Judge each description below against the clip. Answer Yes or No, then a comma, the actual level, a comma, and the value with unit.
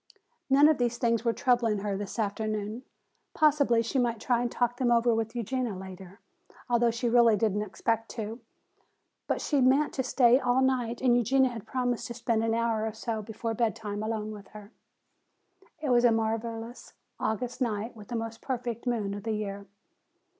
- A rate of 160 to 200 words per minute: Yes, average, 185 wpm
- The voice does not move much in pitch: Yes, narrow, 2.1 semitones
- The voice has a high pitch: Yes, high, 230 Hz